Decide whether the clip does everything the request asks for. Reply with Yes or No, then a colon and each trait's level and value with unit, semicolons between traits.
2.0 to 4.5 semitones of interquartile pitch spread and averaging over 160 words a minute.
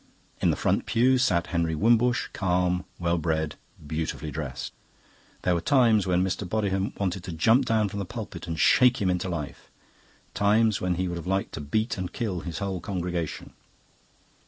Yes: average, 3.8 semitones; average, 180 wpm